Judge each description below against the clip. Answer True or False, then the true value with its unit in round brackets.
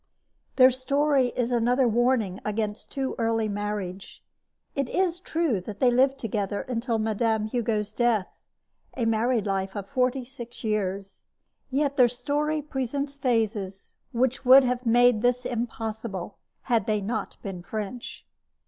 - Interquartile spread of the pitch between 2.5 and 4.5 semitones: True (3.4 semitones)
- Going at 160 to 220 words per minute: False (140 wpm)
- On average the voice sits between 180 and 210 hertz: False (235 Hz)